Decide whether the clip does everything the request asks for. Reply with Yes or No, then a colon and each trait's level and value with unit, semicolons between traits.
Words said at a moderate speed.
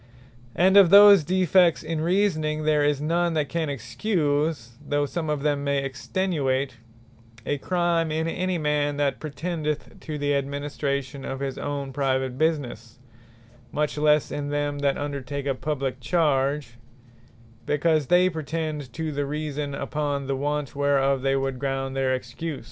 Yes: average, 150 wpm